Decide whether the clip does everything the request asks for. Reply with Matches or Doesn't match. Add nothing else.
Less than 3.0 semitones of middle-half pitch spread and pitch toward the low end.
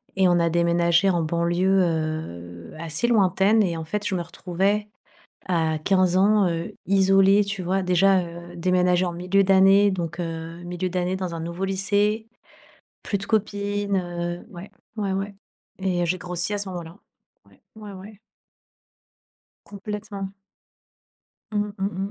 Doesn't match